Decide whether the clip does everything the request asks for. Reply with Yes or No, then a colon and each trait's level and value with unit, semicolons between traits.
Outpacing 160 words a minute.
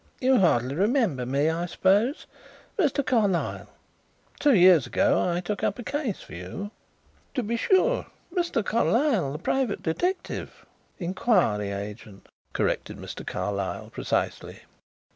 No: slow, 135 wpm